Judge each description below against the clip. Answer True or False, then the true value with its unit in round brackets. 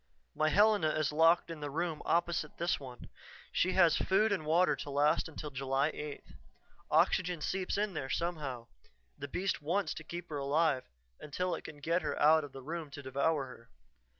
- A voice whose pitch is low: False (155 Hz)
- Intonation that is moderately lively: True (3.4 semitones)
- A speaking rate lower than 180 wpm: False (185 wpm)